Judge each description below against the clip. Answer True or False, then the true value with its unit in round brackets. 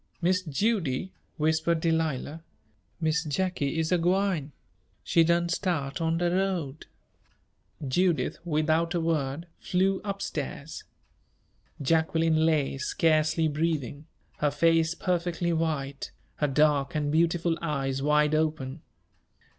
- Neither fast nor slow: False (115 wpm)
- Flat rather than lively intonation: True (2.3 semitones)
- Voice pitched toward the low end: False (160 Hz)